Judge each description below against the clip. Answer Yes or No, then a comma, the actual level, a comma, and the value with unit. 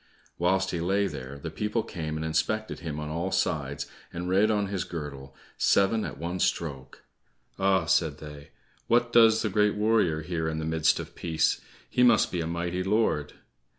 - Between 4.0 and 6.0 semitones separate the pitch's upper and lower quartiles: Yes, average, 4.7 semitones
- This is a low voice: Yes, very low, 85 Hz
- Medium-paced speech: Yes, average, 185 wpm